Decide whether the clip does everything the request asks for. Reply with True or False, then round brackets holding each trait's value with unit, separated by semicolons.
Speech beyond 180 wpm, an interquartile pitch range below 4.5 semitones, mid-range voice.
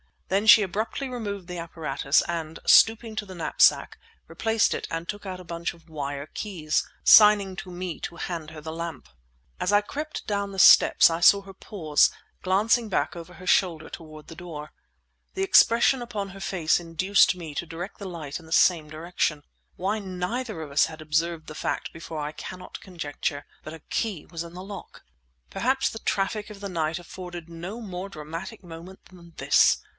True (190 wpm; 3.7 semitones; 175 Hz)